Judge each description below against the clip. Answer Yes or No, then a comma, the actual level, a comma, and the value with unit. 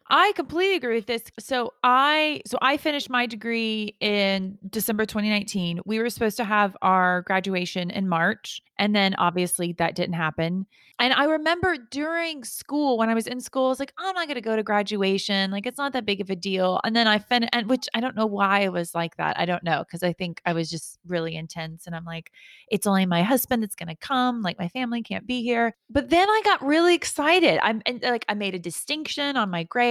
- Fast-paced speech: Yes, fast, 230 wpm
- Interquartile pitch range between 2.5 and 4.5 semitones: No, wide, 5.6 semitones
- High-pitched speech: Yes, high, 220 Hz